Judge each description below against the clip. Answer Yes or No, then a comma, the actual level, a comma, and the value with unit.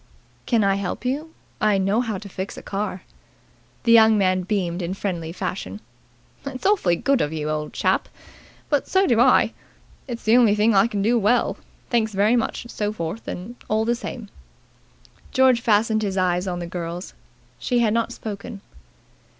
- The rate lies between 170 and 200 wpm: Yes, average, 175 wpm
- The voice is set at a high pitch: Yes, high, 210 Hz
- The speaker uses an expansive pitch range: No, average, 4.0 semitones